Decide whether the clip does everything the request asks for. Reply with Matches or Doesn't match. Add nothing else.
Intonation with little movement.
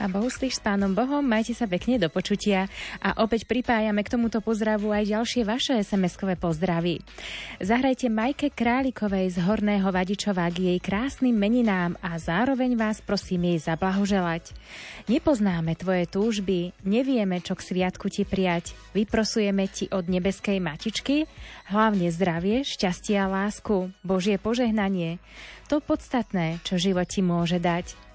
Doesn't match